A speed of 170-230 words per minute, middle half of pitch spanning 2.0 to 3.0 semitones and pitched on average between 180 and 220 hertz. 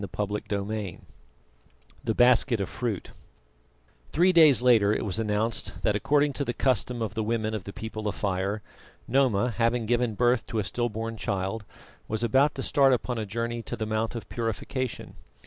No: average, 180 wpm; average, 2.7 semitones; low, 115 Hz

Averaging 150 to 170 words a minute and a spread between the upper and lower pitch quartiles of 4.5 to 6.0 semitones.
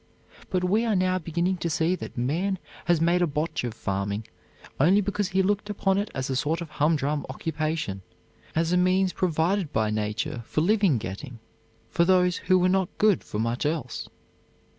No: average, 185 wpm; average, 5.0 semitones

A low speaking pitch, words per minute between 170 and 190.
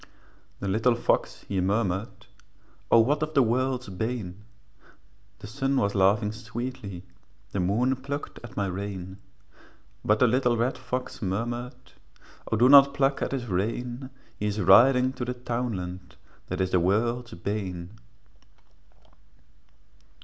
No: low, 115 Hz; slow, 135 wpm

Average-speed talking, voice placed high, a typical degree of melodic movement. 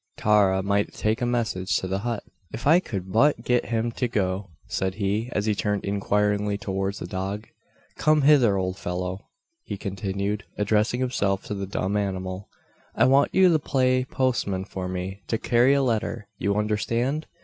No: average, 175 wpm; low, 105 Hz; average, 3.7 semitones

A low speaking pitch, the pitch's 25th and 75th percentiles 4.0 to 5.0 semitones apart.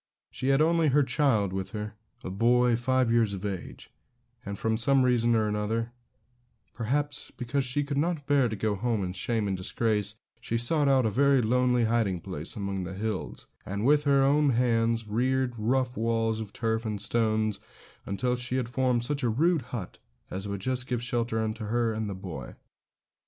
No: low, 115 Hz; average, 3.4 semitones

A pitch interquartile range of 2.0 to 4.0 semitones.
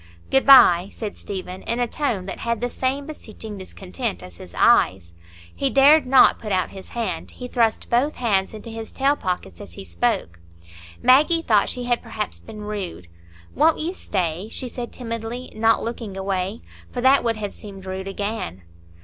No: average, 4.6 semitones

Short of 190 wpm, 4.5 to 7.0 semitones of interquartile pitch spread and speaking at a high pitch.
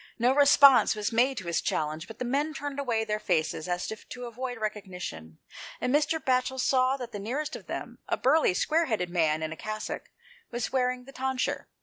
No: fast, 205 wpm; average, 5.1 semitones; high, 240 Hz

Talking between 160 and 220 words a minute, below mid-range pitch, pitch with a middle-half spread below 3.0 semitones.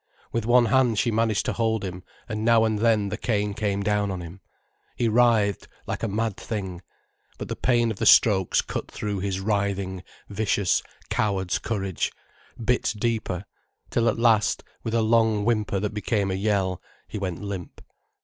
Yes: average, 175 wpm; low, 105 Hz; narrow, 2.5 semitones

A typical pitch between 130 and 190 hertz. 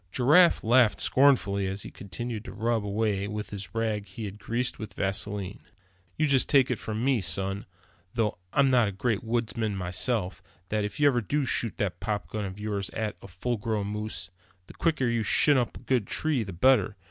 No: low, 110 Hz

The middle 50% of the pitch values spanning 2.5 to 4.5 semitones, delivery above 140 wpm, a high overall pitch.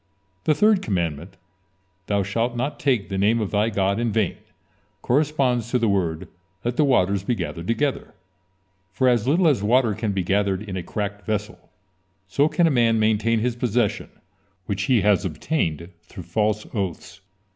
No: average, 3.9 semitones; average, 170 wpm; low, 110 Hz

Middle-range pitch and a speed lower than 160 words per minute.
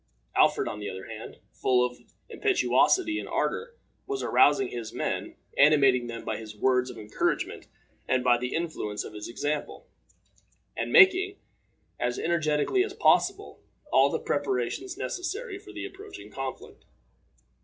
Yes: medium, 145 Hz; average, 145 wpm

